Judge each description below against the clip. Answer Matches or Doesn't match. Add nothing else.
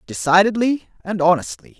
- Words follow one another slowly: Matches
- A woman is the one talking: Doesn't match